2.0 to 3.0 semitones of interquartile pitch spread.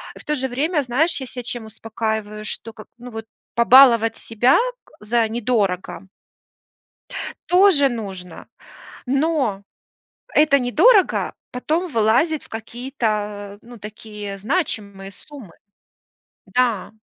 No: average, 4.3 semitones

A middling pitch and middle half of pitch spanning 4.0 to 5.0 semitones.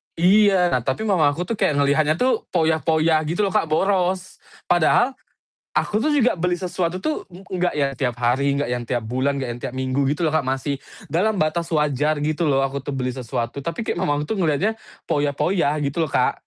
Yes: medium, 155 Hz; average, 4.5 semitones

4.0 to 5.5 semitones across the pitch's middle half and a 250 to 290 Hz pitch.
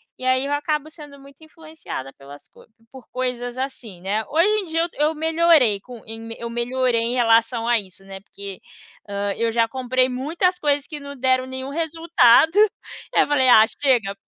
Yes: average, 4.4 semitones; very high, 255 Hz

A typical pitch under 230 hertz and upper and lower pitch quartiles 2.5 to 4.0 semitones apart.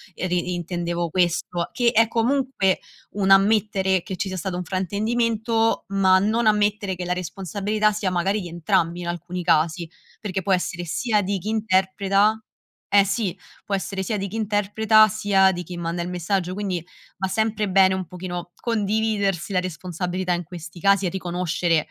Yes: high, 190 Hz; average, 2.8 semitones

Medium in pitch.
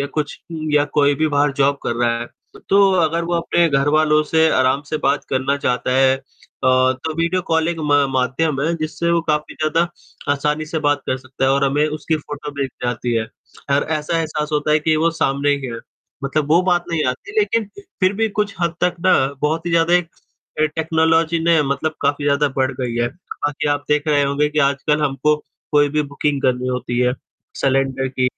Yes: medium, 150 Hz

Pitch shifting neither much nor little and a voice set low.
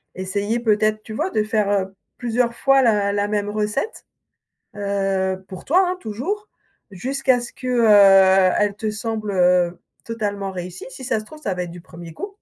No: average, 3.6 semitones; high, 210 Hz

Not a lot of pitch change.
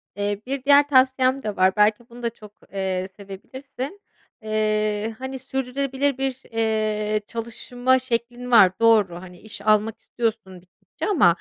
No: average, 3.8 semitones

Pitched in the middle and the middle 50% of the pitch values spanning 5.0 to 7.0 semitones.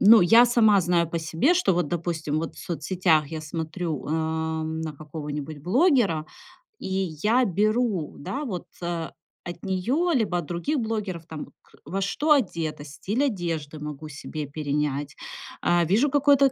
Yes: medium, 175 Hz; wide, 5.5 semitones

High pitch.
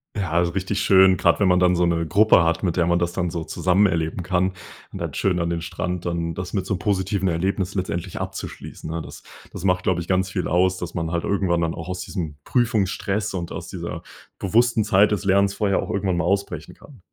No: very low, 90 Hz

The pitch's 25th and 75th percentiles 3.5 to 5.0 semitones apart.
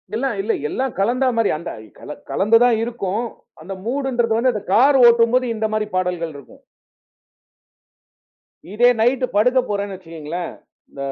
Yes: average, 4.2 semitones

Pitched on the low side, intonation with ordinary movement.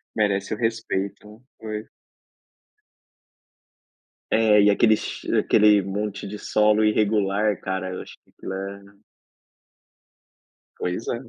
No: low, 105 Hz; narrow, 1.5 semitones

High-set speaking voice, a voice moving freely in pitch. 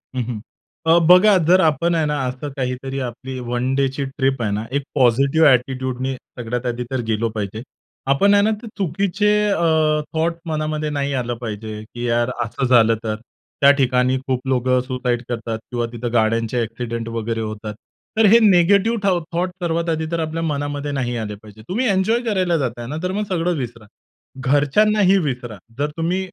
No: low, 135 Hz; wide, 5.7 semitones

